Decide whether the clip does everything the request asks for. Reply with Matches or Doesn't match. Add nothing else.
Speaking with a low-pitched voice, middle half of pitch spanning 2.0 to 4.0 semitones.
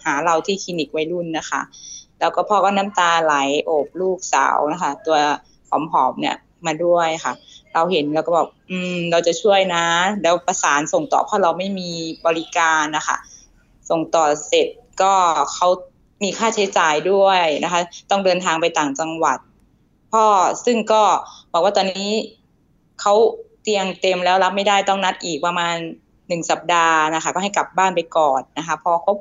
Doesn't match